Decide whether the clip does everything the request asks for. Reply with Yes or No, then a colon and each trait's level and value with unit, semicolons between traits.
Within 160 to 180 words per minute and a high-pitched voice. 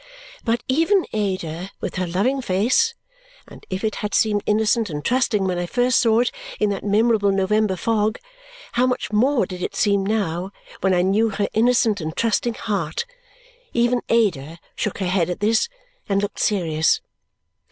Yes: average, 170 wpm; high, 210 Hz